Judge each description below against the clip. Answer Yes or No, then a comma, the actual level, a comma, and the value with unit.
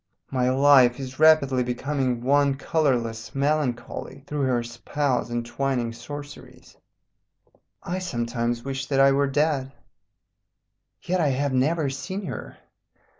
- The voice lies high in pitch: No, low, 135 Hz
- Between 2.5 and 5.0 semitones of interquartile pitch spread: Yes, average, 2.8 semitones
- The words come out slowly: Yes, slow, 125 wpm